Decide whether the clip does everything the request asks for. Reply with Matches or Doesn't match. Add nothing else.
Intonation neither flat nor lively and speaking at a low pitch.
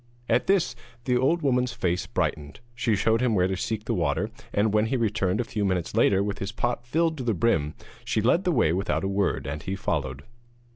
Matches